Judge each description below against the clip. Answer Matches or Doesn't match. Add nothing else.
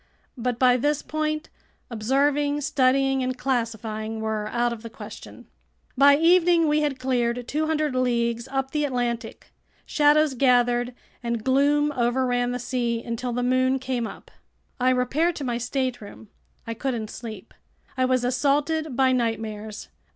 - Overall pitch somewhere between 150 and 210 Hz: Doesn't match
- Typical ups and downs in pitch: Matches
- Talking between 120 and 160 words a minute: Matches